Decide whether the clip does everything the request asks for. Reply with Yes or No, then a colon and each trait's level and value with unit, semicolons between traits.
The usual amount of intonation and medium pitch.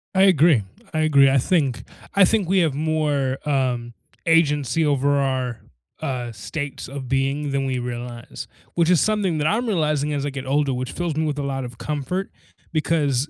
Yes: average, 3.2 semitones; medium, 145 Hz